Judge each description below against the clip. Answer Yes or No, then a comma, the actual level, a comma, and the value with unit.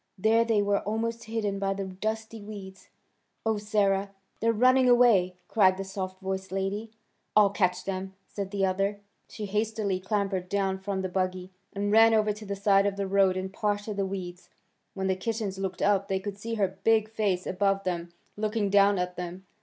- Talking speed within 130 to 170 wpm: No, average, 190 wpm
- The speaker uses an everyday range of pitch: No, narrow, 1.9 semitones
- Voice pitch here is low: No, high, 200 Hz